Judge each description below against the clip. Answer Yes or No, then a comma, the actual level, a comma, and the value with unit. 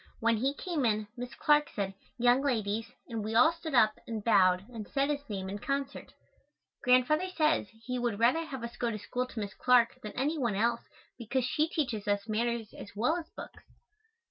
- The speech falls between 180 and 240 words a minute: Yes, average, 200 wpm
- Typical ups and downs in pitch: Yes, average, 4.4 semitones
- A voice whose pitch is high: Yes, high, 240 Hz